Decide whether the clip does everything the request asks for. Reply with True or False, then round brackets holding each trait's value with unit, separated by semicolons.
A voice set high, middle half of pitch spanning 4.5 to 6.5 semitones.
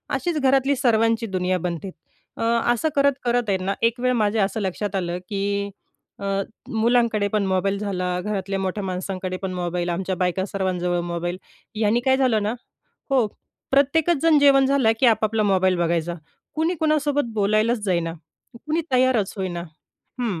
True (205 Hz; 4.9 semitones)